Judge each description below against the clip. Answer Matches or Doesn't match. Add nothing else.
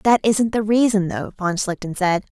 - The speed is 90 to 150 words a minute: Doesn't match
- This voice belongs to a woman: Matches